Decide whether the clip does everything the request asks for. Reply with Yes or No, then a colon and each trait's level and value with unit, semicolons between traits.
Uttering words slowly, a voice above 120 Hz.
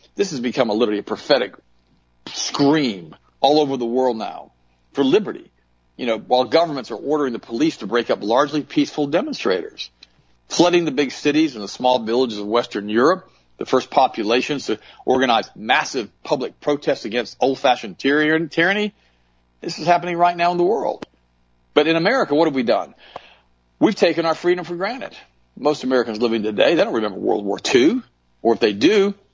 No: average, 175 wpm; medium, 140 Hz